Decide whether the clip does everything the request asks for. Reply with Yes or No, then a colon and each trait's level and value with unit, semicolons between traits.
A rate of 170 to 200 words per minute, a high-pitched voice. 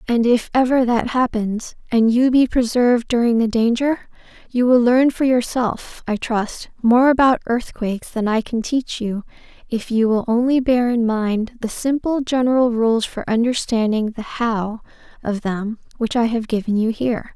Yes: average, 175 wpm; high, 235 Hz